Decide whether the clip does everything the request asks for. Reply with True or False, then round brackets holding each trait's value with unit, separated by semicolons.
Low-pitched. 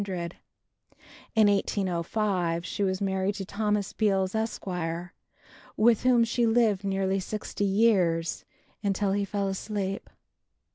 False (200 Hz)